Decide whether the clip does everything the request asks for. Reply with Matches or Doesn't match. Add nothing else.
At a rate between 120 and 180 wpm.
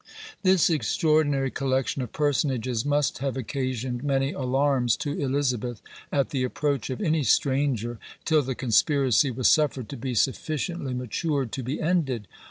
Matches